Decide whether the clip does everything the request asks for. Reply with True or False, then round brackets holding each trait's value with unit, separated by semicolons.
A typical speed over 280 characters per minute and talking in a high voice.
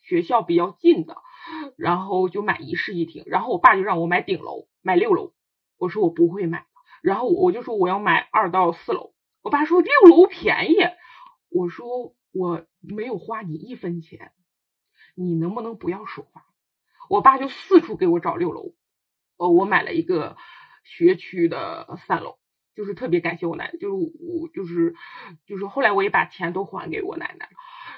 False (255 characters per minute; 320 Hz)